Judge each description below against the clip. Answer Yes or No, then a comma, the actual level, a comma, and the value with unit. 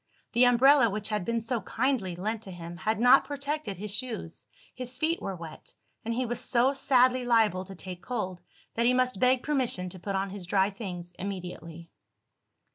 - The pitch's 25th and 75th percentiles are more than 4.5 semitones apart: Yes, average, 5.1 semitones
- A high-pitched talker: Yes, high, 220 Hz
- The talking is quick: No, average, 190 wpm